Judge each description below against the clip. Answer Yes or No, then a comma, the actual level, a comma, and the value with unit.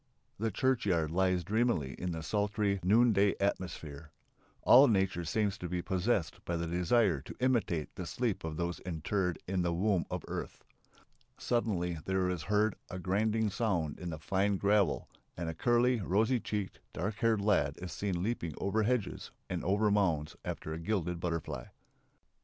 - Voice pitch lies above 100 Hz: No, very low, 95 Hz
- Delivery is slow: No, average, 165 wpm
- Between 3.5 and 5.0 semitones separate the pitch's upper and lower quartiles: Yes, average, 3.8 semitones